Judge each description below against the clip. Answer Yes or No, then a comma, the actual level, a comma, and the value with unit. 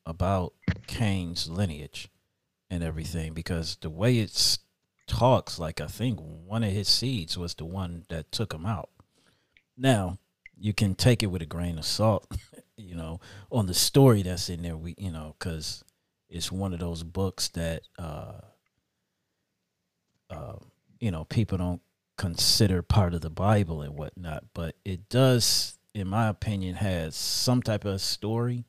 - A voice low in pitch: Yes, very low, 95 Hz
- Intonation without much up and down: No, average, 3.9 semitones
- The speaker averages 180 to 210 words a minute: No, average, 160 wpm